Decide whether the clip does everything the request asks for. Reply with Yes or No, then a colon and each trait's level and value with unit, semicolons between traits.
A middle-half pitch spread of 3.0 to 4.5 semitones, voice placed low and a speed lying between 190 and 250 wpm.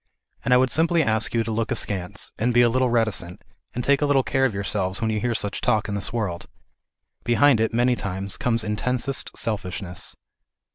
Yes: average, 3.4 semitones; low, 115 Hz; average, 200 wpm